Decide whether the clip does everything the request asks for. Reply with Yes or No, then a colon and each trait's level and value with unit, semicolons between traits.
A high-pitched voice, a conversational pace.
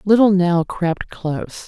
No: medium, 180 Hz; average, 145 wpm